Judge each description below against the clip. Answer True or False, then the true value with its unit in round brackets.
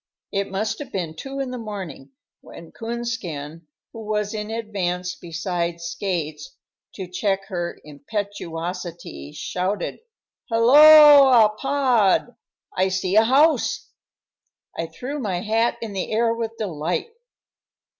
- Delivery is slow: True (120 wpm)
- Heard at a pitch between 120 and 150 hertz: False (200 Hz)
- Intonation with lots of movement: False (4.7 semitones)